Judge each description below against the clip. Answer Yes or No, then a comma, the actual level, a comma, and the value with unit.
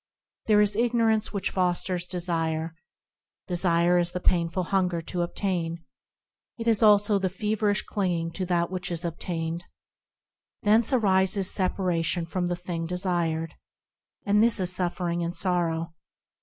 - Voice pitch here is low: No, medium, 180 Hz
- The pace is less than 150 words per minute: Yes, slow, 135 wpm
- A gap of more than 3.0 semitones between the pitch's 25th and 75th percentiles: No, average, 2.7 semitones